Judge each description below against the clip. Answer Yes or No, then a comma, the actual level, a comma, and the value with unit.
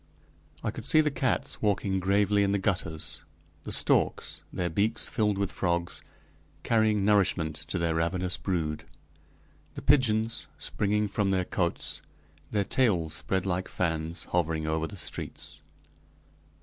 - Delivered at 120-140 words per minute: Yes, slow, 135 wpm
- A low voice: Yes, very low, 95 Hz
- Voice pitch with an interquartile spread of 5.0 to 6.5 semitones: No, average, 3.5 semitones